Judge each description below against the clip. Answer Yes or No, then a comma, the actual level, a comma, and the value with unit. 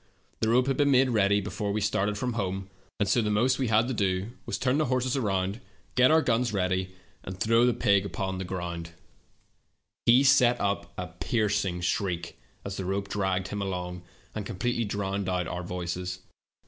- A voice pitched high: No, low, 100 Hz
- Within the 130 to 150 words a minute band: No, average, 160 wpm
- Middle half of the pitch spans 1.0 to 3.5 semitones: No, average, 4.2 semitones